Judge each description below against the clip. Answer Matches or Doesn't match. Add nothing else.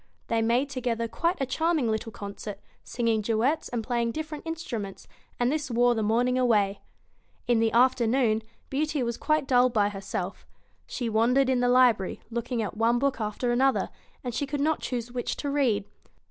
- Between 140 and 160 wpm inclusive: Doesn't match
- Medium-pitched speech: Doesn't match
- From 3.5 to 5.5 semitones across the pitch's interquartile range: Doesn't match